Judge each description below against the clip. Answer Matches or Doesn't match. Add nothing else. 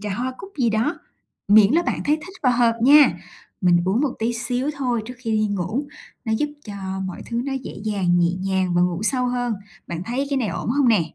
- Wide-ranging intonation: Doesn't match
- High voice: Matches